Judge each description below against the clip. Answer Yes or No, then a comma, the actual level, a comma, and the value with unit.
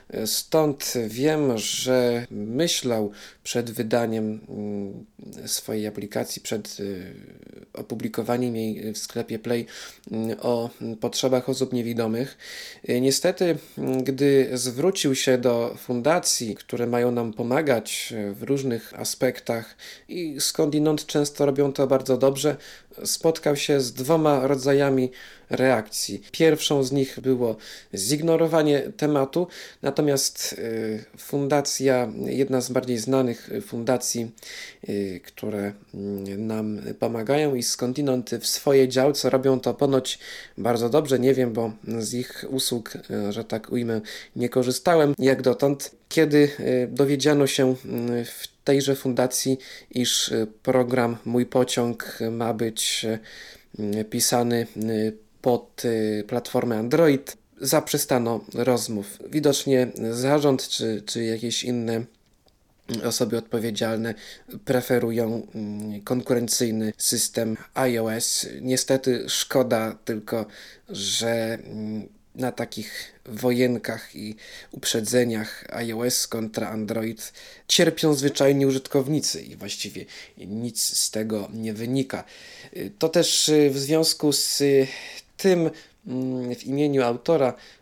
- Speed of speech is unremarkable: No, slow, 100 wpm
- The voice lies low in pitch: Yes, low, 125 Hz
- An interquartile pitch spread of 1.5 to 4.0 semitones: Yes, average, 3.4 semitones